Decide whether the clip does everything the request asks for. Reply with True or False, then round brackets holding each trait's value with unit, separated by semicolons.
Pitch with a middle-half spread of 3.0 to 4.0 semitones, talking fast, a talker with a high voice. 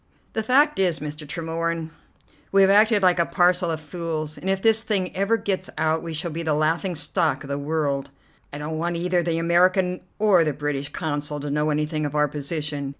False (3.4 semitones; 210 wpm; 165 Hz)